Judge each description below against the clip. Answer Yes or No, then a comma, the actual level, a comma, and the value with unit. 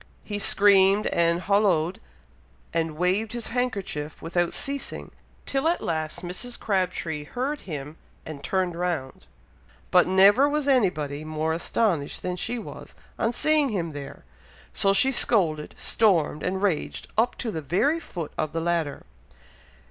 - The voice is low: No, medium, 180 Hz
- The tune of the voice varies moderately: No, wide, 5.7 semitones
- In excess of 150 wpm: No, average, 140 wpm